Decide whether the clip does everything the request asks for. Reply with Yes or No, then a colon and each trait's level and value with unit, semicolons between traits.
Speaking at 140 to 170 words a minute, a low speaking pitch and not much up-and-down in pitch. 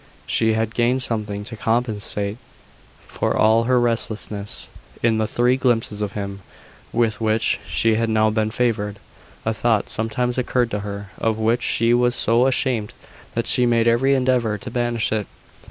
Yes: average, 165 wpm; low, 115 Hz; narrow, 2.0 semitones